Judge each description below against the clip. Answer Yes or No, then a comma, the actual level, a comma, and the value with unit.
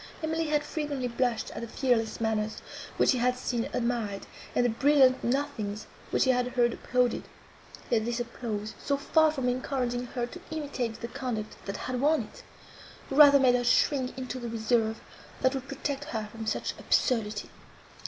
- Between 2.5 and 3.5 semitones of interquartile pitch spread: Yes, average, 3.1 semitones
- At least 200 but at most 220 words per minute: No, average, 175 wpm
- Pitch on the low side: No, very high, 250 Hz